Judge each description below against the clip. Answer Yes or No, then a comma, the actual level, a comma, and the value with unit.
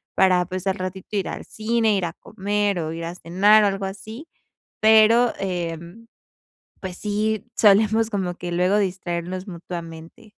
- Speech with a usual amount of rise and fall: Yes, average, 3.3 semitones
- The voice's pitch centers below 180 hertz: No, high, 195 Hz